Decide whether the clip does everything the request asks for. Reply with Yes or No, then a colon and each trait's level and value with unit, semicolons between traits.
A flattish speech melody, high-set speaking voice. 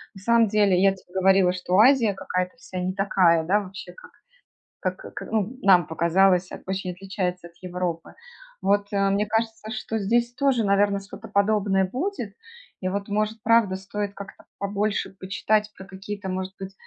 Yes: narrow, 2.3 semitones; high, 195 Hz